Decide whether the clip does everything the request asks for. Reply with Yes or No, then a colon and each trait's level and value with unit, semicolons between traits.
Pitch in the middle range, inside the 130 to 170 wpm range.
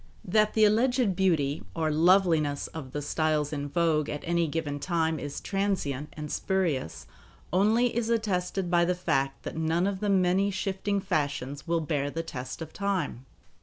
Yes: medium, 170 Hz; average, 165 wpm